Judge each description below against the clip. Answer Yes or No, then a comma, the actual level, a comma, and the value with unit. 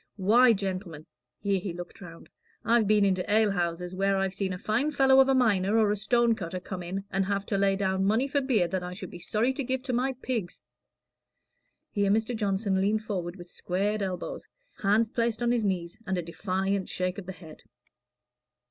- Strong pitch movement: No, average, 3.3 semitones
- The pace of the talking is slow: No, fast, 205 wpm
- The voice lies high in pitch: Yes, high, 200 Hz